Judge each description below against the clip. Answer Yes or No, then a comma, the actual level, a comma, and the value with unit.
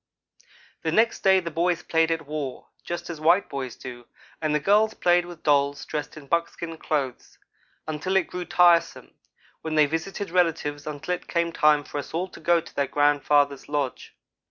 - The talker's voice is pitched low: No, medium, 160 Hz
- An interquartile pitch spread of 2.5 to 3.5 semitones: Yes, average, 3.1 semitones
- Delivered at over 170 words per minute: Yes, average, 180 wpm